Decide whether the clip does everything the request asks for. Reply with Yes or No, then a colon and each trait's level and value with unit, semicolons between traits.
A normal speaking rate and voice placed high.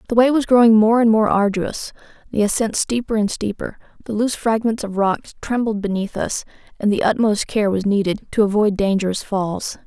Yes: average, 190 wpm; high, 215 Hz